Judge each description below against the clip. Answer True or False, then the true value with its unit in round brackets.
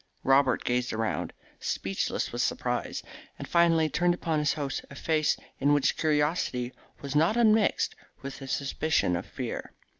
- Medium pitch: True (145 Hz)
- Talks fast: False (155 wpm)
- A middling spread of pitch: True (3.4 semitones)